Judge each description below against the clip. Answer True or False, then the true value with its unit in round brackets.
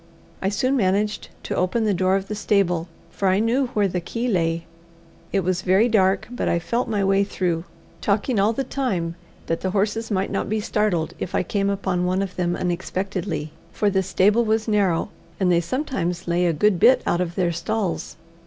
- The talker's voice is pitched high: True (195 Hz)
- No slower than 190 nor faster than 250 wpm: True (200 wpm)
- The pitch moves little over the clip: False (3.1 semitones)